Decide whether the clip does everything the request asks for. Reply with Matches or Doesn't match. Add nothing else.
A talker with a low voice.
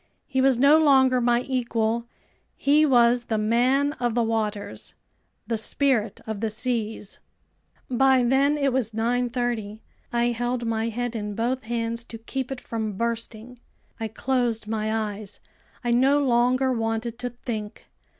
Doesn't match